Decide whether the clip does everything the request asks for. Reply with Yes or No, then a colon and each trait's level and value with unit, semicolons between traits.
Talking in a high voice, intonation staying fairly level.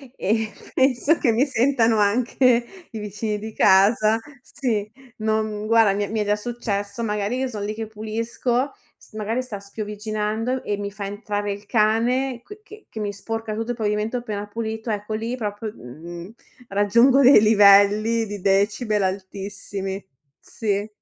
Yes: high, 215 Hz; narrow, 2.2 semitones